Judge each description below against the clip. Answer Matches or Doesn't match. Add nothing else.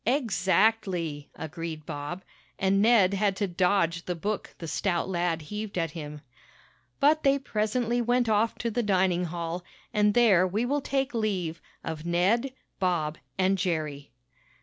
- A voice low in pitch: Doesn't match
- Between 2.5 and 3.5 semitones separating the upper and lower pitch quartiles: Doesn't match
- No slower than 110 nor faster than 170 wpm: Matches